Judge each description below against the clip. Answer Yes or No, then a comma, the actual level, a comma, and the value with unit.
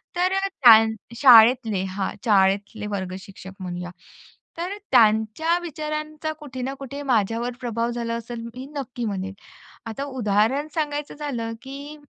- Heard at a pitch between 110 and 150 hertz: No, high, 240 Hz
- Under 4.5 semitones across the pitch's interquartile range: No, average, 5.3 semitones